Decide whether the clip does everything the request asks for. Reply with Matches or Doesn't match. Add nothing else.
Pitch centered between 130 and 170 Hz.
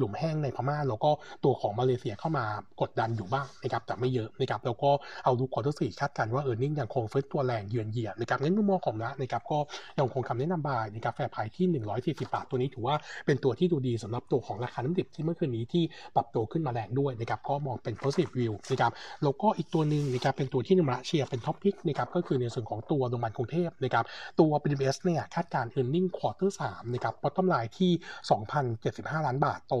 Matches